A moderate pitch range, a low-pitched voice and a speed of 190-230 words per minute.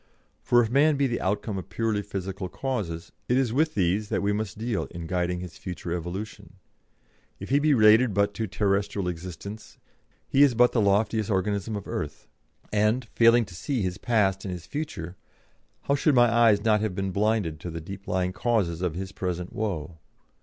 Yes: average, 4.0 semitones; low, 100 Hz; average, 195 wpm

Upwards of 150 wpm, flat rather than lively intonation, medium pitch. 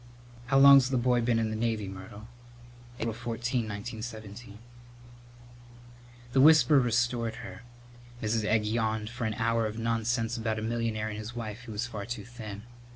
No: average, 160 wpm; narrow, 1.8 semitones; low, 115 Hz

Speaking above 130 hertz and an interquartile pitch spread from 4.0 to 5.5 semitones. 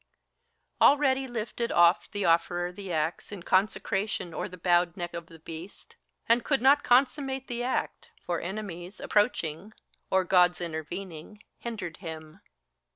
Yes: medium, 185 Hz; average, 5.0 semitones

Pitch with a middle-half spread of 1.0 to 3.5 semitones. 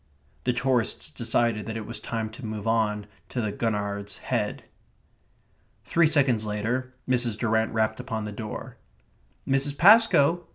Yes: average, 3.2 semitones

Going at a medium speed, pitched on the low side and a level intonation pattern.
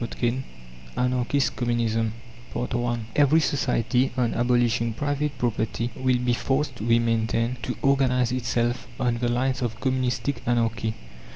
No: slow, 130 wpm; low, 120 Hz; narrow, 1.7 semitones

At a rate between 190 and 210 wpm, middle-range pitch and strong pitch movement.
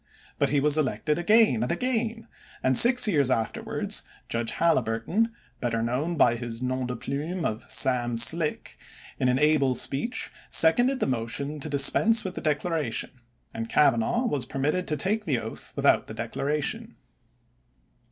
No: average, 150 wpm; medium, 145 Hz; wide, 6.0 semitones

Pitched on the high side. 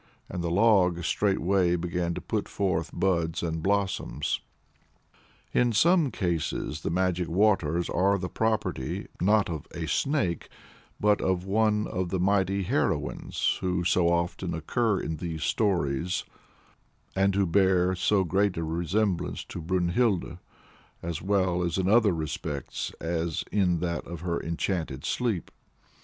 No: very low, 90 Hz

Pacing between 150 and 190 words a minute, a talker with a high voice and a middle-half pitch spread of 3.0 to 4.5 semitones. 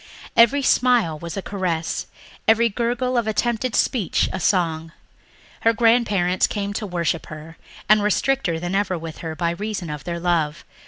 No: average, 165 wpm; high, 195 Hz; average, 5.3 semitones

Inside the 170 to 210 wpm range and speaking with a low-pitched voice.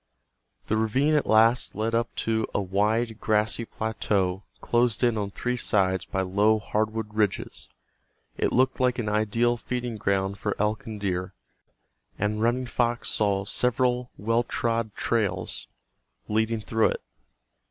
No: average, 140 wpm; low, 110 Hz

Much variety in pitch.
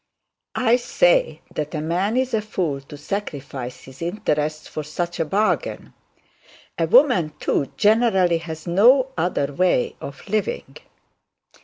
Yes: wide, 6.1 semitones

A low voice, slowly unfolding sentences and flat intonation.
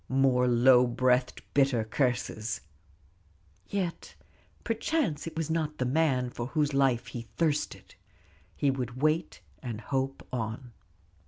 No: low, 130 Hz; slow, 120 wpm; average, 3.5 semitones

